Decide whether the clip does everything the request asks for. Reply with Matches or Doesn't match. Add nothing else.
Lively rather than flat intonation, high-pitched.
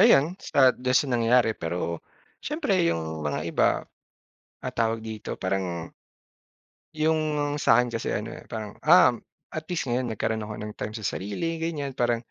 Doesn't match